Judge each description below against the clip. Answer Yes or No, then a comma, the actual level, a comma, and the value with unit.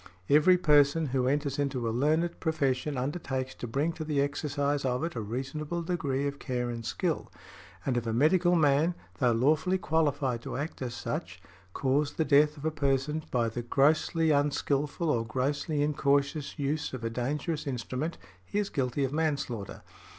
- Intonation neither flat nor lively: Yes, average, 3.1 semitones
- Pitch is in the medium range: Yes, medium, 145 Hz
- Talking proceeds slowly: No, average, 175 wpm